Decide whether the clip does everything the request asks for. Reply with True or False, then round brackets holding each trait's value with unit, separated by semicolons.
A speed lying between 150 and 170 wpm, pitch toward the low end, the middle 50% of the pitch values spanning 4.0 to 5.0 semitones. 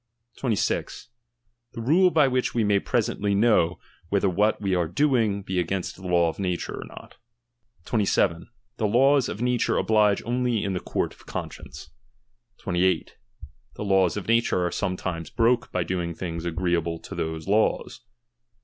True (160 wpm; 100 Hz; 4.7 semitones)